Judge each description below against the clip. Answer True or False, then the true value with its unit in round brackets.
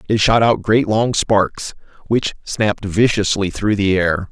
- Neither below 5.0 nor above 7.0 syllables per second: False (4.1 syllables/s)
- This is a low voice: True (105 Hz)